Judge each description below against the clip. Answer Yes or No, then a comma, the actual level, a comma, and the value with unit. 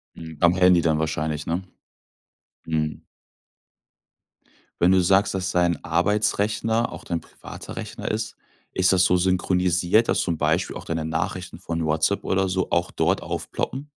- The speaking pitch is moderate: No, very low, 90 Hz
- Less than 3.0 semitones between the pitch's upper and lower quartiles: Yes, narrow, 2.5 semitones